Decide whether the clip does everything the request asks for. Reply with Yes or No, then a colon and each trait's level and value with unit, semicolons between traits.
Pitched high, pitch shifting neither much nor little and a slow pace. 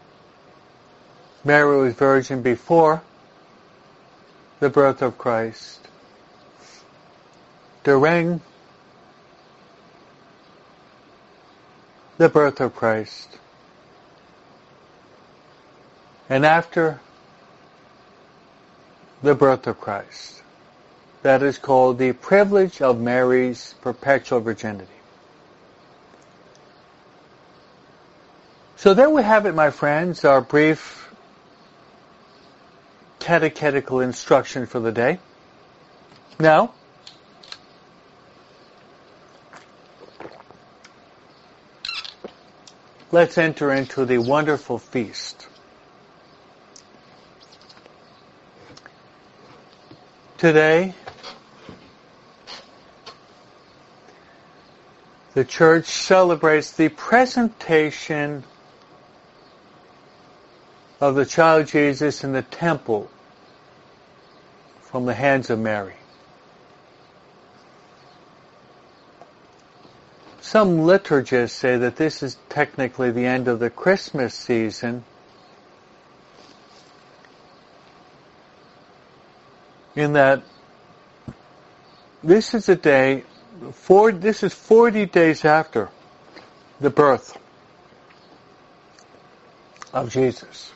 No: medium, 140 Hz; average, 4.3 semitones; slow, 65 wpm